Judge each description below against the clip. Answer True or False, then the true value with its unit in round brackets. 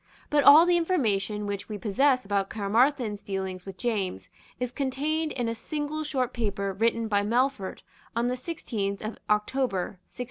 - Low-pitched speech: False (230 Hz)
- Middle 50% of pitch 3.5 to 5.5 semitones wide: True (5.2 semitones)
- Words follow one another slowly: False (165 wpm)